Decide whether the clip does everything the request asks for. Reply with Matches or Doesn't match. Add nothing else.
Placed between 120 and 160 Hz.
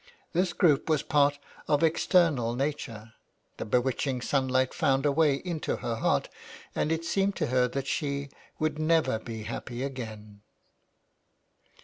Matches